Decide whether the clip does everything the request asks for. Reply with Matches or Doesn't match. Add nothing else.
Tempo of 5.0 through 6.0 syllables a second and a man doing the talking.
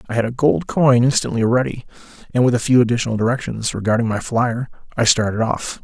Doesn't match